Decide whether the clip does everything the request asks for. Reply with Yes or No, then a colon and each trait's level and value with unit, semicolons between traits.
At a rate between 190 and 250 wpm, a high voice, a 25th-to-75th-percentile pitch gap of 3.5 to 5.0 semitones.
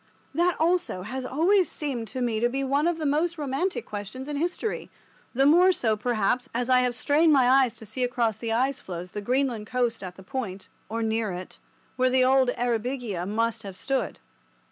Yes: average, 195 wpm; very high, 250 Hz; average, 3.9 semitones